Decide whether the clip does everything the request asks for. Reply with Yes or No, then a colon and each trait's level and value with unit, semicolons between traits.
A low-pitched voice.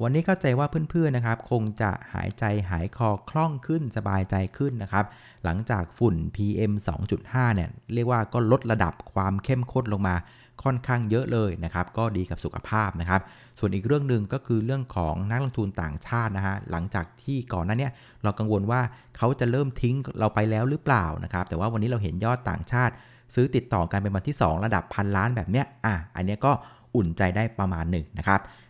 Yes: low, 110 Hz